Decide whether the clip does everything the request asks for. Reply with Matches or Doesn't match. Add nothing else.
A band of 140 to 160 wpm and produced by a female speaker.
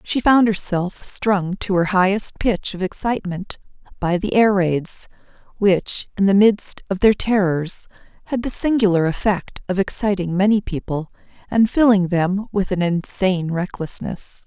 Matches